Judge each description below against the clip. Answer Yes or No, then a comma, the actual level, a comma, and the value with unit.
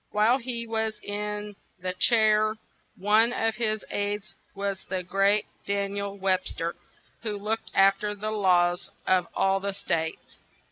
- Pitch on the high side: Yes, high, 205 Hz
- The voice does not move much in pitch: Yes, narrow, 1.8 semitones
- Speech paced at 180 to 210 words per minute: No, average, 150 wpm